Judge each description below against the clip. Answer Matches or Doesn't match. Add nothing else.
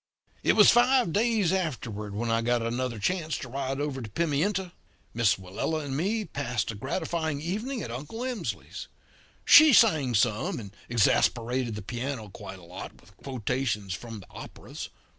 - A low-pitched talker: Matches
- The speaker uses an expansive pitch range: Matches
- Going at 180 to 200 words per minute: Doesn't match